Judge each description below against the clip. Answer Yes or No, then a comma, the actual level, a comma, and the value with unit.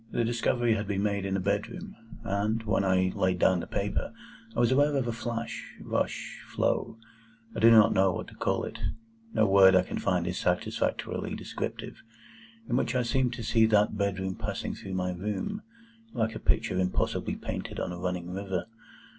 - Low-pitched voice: Yes, low, 105 Hz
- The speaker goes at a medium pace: Yes, average, 170 wpm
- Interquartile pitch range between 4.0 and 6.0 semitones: No, average, 3.2 semitones